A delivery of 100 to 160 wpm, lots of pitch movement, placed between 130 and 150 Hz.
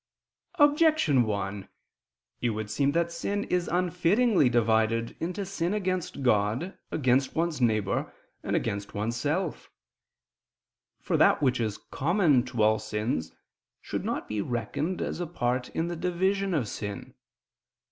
Yes: slow, 135 wpm; wide, 8.2 semitones; medium, 140 Hz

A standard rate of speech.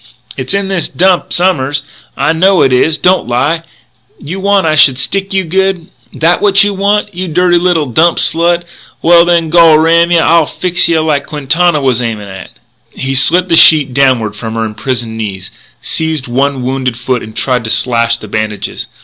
Yes: average, 190 wpm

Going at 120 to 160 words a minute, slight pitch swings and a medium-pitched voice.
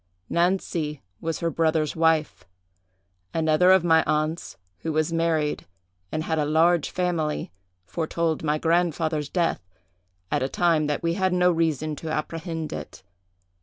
Yes: average, 140 wpm; narrow, 1.6 semitones; medium, 160 Hz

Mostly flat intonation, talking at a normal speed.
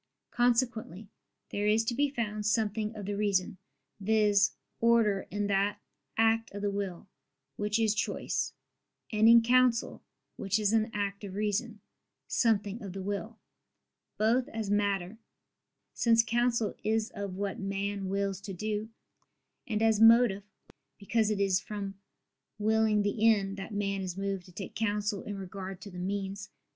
Yes: narrow, 2.0 semitones; average, 150 wpm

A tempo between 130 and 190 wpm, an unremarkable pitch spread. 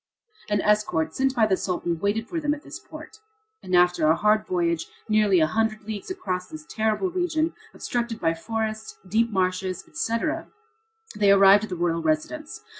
Yes: average, 175 wpm; average, 4.2 semitones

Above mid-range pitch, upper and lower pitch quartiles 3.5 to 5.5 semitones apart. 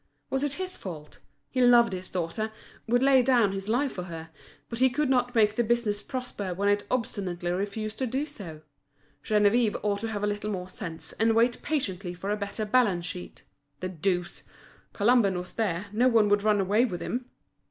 Yes: high, 210 Hz; average, 4.5 semitones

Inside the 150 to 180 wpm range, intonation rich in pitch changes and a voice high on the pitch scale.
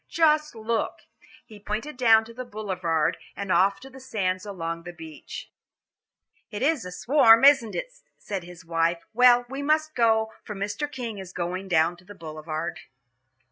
Yes: average, 170 wpm; wide, 6.0 semitones; high, 210 Hz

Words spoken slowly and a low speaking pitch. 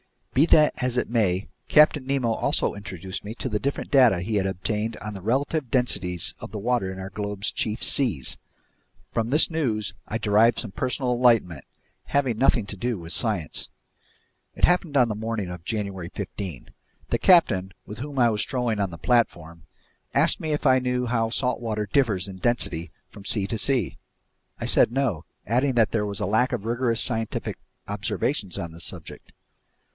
No: average, 180 wpm; low, 110 Hz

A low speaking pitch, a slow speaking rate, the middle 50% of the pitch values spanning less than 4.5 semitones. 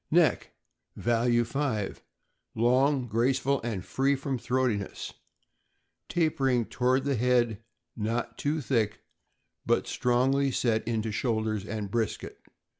Yes: low, 120 Hz; slow, 110 wpm; average, 3.2 semitones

